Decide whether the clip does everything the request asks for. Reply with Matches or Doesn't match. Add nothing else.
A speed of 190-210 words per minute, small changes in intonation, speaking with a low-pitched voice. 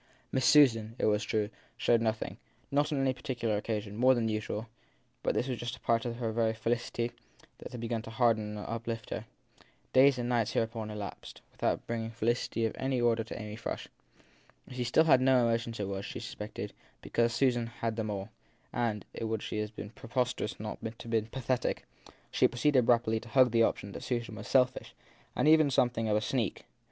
Matches